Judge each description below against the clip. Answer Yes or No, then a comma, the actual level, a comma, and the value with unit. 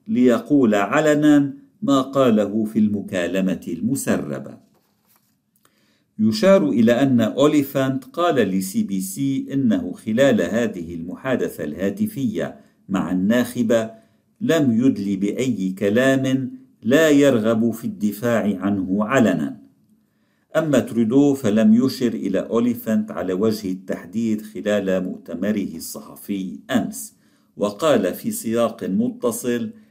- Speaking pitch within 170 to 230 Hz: No, low, 120 Hz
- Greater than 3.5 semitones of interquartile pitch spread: Yes, average, 5.0 semitones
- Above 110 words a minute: No, average, 100 wpm